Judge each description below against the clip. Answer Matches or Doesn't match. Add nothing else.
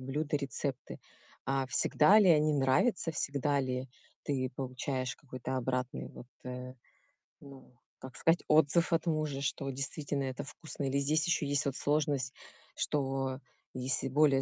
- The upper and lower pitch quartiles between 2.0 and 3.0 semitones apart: Matches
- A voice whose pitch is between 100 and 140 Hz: Matches